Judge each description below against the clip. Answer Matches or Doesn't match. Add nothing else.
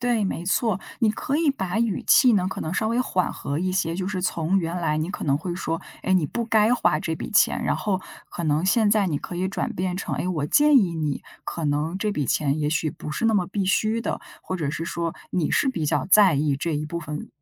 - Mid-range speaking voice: Matches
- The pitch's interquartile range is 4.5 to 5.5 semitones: Matches